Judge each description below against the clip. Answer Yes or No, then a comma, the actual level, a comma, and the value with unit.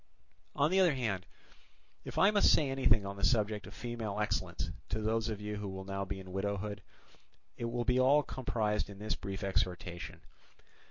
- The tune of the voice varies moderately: Yes, average, 3.5 semitones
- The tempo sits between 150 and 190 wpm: Yes, average, 185 wpm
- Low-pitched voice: Yes, low, 105 Hz